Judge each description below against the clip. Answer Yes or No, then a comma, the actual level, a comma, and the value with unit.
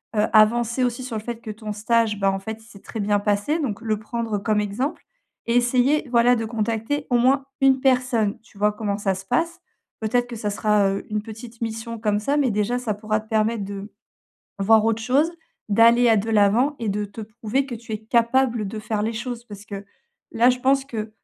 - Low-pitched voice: No, high, 225 Hz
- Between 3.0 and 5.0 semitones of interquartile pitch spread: No, narrow, 2.6 semitones